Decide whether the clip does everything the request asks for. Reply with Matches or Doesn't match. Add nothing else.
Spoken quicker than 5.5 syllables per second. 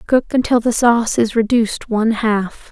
Doesn't match